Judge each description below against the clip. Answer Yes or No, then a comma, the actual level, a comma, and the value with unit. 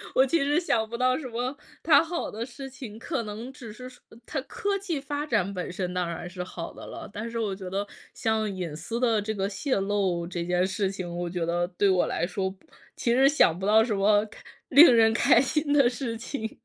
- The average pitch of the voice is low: No, high, 220 Hz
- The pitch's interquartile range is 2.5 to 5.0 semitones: No, wide, 5.4 semitones